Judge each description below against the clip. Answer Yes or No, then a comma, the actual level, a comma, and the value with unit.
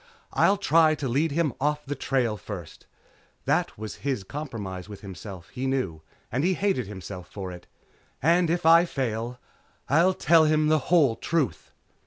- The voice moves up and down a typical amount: No, wide, 7.3 semitones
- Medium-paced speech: Yes, average, 170 wpm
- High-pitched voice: No, low, 135 Hz